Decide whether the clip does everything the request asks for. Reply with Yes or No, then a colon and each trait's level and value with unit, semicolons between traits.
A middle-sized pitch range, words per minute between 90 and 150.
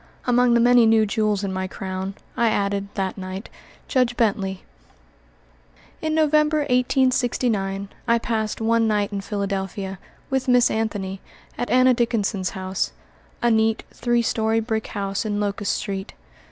Yes: average, 3.5 semitones; average, 140 wpm